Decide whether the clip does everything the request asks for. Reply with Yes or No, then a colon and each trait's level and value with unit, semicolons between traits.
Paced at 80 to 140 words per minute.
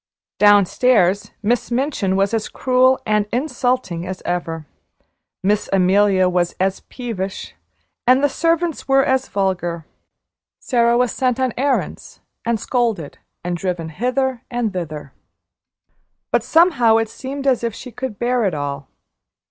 Yes: slow, 135 wpm